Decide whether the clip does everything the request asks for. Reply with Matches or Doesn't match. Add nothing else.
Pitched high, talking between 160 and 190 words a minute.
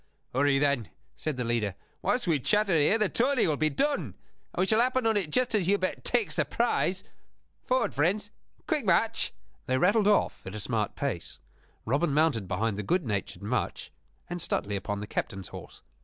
Doesn't match